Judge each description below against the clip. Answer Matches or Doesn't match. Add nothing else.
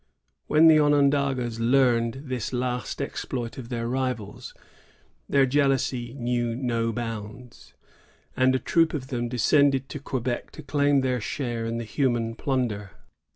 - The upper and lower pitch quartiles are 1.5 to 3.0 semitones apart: Matches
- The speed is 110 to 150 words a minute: Matches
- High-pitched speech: Doesn't match